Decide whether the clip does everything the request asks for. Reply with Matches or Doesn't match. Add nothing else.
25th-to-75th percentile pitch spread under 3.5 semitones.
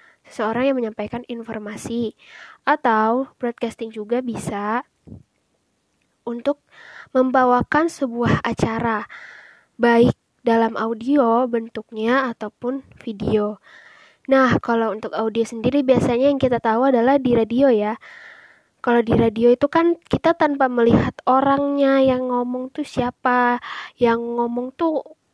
Matches